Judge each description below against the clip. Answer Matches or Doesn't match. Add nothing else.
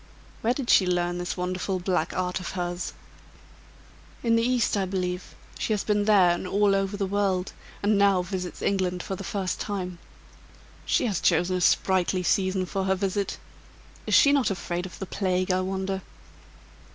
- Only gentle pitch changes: Matches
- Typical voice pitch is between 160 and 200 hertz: Matches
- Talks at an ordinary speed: Matches